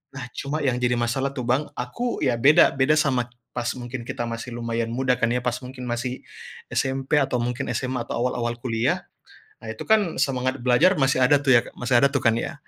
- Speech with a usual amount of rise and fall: No, narrow, 2.0 semitones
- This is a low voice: Yes, low, 125 Hz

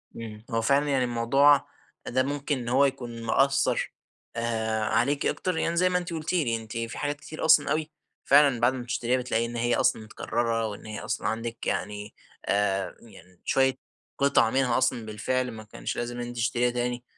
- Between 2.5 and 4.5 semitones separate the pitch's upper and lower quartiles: Yes, average, 3.4 semitones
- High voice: No, low, 120 Hz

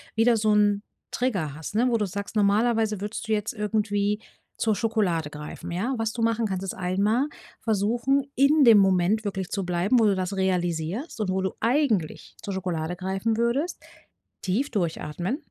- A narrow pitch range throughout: No, average, 3.5 semitones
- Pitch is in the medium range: No, high, 205 Hz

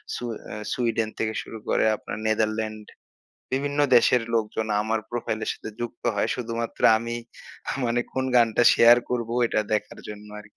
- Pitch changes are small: Yes, narrow, 1.6 semitones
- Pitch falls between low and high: No, low, 115 Hz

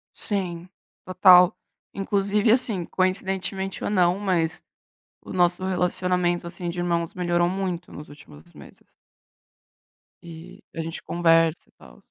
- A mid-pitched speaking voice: Yes, medium, 180 Hz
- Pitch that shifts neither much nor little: No, narrow, 1.8 semitones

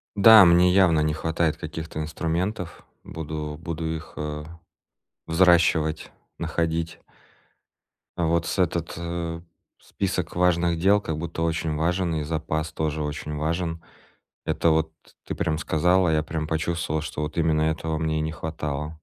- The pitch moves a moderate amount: No, narrow, 1.6 semitones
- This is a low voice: Yes, very low, 80 Hz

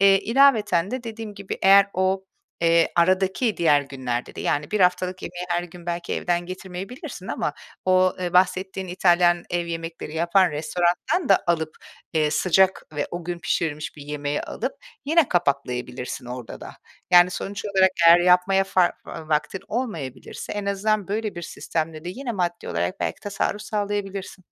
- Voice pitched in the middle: Yes, medium, 180 Hz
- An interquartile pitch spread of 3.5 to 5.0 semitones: No, average, 2.8 semitones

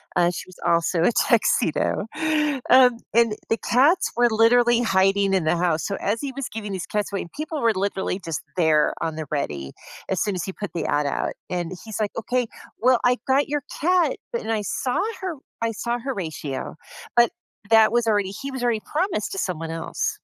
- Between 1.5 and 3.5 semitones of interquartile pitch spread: No, wide, 5.6 semitones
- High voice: Yes, high, 215 Hz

